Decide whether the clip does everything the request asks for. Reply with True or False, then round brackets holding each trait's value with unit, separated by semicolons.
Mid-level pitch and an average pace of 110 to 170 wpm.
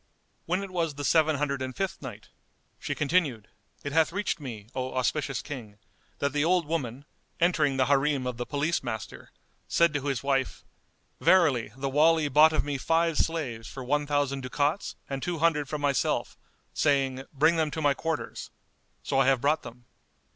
False (145 Hz; 180 wpm)